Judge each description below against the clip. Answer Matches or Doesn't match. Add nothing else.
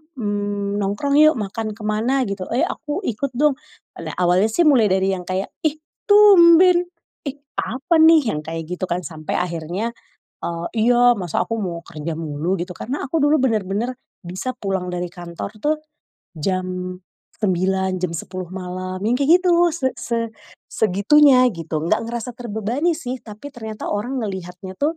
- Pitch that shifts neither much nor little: Doesn't match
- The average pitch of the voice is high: Matches